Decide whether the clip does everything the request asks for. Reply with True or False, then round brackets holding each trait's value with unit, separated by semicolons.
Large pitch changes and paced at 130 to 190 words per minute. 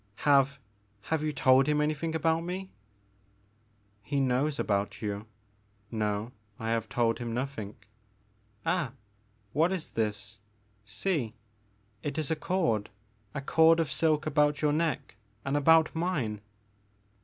True (6.5 semitones; 150 wpm)